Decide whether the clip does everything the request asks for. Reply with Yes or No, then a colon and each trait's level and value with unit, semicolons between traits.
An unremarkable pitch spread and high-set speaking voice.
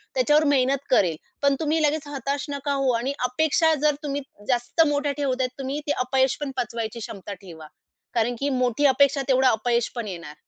Yes: average, 3.1 semitones; very high, 265 Hz